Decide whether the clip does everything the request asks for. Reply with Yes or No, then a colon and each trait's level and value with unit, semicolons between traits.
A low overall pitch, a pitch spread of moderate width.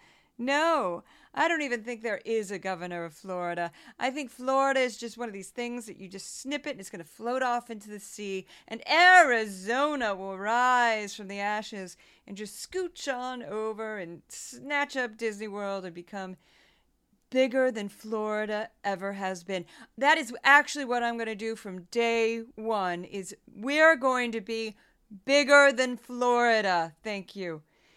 No: high, 225 Hz; average, 4.2 semitones